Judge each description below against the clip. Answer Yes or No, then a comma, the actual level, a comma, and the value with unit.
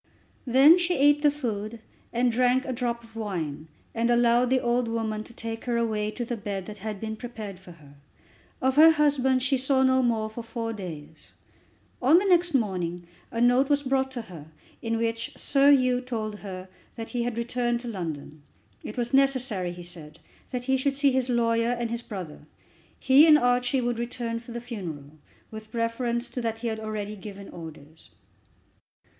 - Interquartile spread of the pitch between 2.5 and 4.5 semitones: Yes, average, 3.3 semitones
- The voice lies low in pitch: No, high, 235 Hz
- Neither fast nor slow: Yes, average, 190 wpm